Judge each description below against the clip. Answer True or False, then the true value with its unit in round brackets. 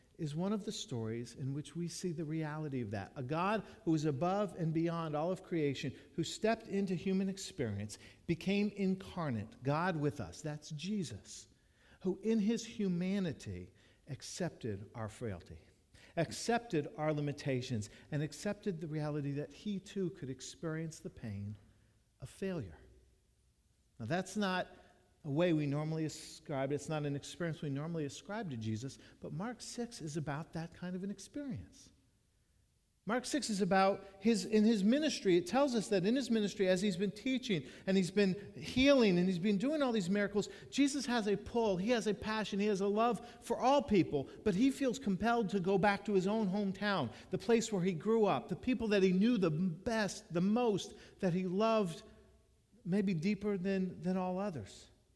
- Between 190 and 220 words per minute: False (180 wpm)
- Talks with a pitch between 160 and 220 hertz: True (185 Hz)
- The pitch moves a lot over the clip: True (6.1 semitones)